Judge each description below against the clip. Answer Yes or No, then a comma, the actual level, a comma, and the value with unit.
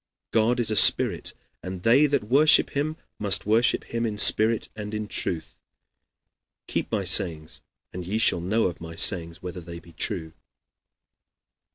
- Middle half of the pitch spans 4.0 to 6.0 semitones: Yes, average, 4.8 semitones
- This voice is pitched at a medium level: No, low, 105 Hz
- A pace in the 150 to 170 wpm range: Yes, average, 160 wpm